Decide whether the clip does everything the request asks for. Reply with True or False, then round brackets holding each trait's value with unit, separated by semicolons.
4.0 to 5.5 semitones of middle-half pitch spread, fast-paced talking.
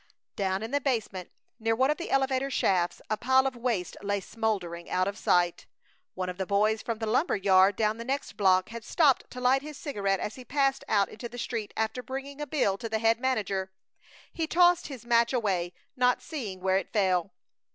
True (5.0 semitones; 210 wpm)